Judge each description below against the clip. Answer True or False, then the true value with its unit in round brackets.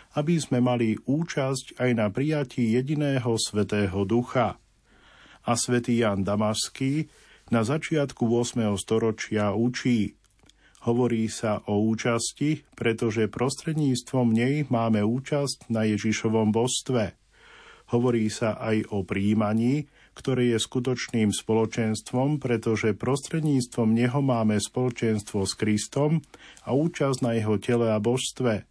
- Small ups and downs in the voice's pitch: False (3.0 semitones)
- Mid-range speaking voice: False (120 Hz)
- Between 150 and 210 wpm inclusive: False (115 wpm)